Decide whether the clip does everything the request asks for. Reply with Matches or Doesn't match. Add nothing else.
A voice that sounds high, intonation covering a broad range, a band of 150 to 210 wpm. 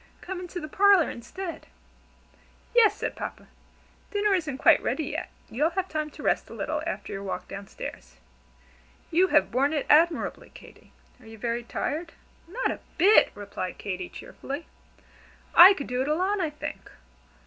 Matches